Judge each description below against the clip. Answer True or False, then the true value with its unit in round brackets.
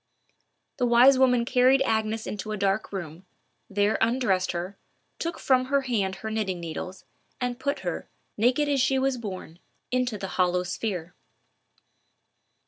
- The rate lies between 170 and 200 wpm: False (145 wpm)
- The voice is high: True (220 Hz)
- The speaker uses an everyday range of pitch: True (5.0 semitones)